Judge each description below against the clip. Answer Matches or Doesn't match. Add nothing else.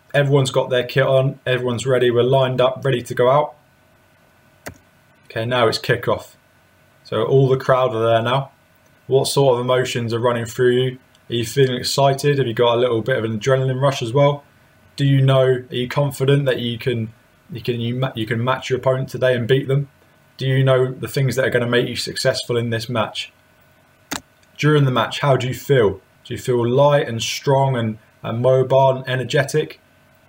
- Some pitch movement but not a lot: Doesn't match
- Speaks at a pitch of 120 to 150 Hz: Matches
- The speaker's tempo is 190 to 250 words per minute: Matches